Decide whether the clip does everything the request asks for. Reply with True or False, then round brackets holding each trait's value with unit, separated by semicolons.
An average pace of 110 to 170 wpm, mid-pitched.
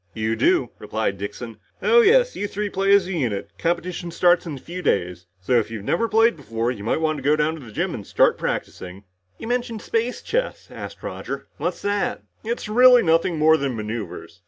False (200 wpm; 170 Hz)